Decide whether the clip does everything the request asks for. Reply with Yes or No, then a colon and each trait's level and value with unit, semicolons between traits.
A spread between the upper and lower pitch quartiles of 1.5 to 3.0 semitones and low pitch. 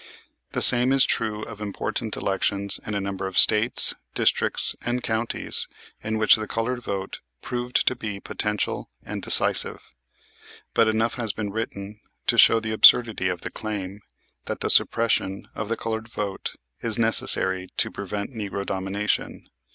Yes: narrow, 2.4 semitones; low, 110 Hz